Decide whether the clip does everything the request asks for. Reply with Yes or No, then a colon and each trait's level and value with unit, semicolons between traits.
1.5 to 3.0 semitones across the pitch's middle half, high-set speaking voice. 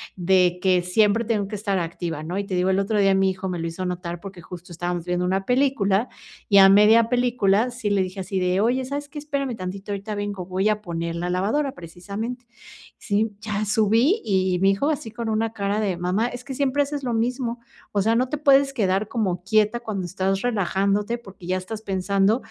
No: average, 3.8 semitones; high, 200 Hz